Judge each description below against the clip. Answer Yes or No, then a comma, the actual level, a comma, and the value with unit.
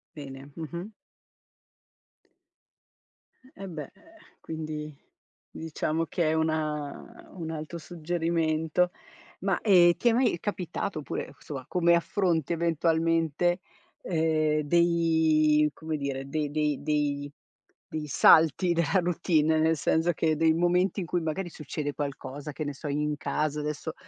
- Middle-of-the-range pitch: Yes, medium, 160 Hz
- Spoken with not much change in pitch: Yes, narrow, 2.1 semitones